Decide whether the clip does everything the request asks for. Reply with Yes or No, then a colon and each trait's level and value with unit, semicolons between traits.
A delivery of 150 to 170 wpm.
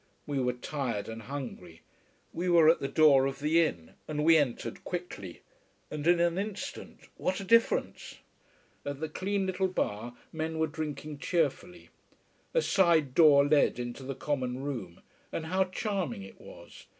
Yes: average, 160 wpm